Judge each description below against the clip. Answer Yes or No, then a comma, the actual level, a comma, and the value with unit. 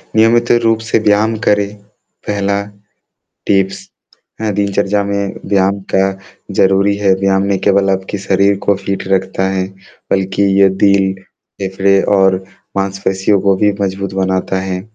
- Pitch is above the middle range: No, low, 100 Hz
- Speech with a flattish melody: Yes, narrow, 0.9 semitones